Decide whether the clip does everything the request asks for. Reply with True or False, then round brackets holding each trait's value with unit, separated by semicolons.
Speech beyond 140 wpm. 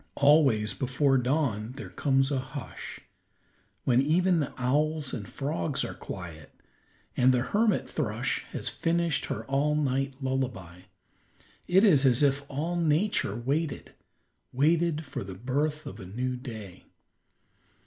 False (135 wpm)